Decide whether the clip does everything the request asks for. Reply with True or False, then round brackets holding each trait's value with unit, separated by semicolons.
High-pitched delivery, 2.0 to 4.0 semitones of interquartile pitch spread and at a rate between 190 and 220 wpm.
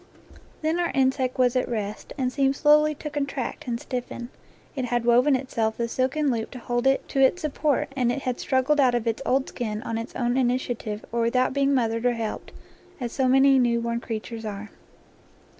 True (250 Hz; 2.6 semitones; 200 wpm)